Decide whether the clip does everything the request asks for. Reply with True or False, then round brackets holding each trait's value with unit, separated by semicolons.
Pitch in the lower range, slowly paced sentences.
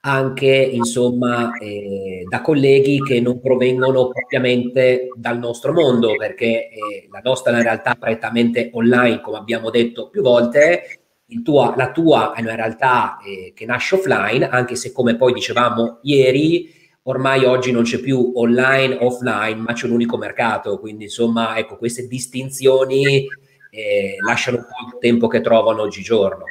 False (125 Hz; 155 wpm)